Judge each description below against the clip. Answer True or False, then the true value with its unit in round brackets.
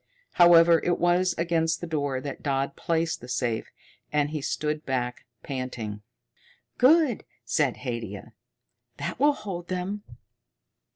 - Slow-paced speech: True (125 wpm)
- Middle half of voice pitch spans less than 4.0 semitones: False (5.0 semitones)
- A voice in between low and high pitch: True (160 Hz)